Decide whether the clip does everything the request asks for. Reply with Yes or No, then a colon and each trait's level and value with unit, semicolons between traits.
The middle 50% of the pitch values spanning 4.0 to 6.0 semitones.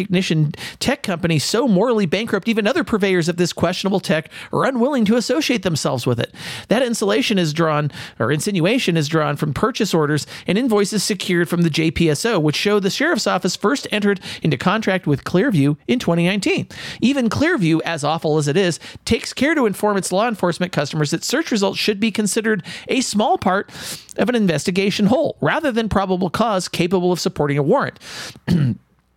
Yes: average, 4.9 semitones